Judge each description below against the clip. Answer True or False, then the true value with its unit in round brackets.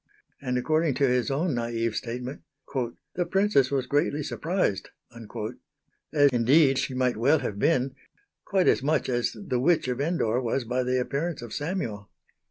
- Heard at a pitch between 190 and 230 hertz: False (130 Hz)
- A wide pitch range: False (4.0 semitones)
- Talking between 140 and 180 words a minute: True (160 wpm)